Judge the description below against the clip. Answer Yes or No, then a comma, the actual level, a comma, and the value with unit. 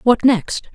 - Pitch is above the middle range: Yes, high, 225 Hz